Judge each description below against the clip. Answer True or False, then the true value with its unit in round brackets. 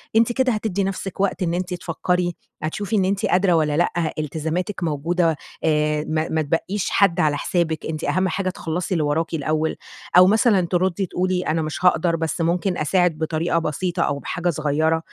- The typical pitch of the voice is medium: True (170 Hz)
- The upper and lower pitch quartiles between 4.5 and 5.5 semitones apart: False (2.8 semitones)